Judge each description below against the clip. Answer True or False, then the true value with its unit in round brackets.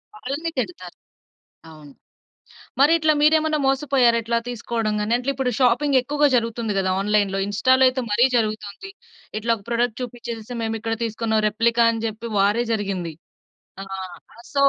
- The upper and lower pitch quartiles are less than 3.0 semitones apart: False (3.4 semitones)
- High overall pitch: True (235 Hz)